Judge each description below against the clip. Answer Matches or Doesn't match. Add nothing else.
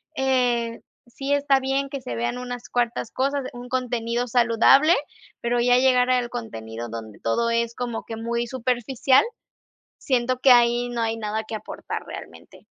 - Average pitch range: Doesn't match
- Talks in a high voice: Matches